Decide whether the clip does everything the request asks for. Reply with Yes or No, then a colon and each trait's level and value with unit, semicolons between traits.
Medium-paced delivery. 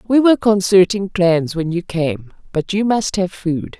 Yes: average, 190 wpm